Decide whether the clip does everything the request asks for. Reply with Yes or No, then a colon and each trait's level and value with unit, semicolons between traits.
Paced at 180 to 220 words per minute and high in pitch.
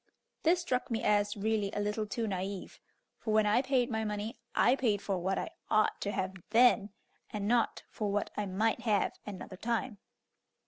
Yes: average, 185 wpm; high, 215 Hz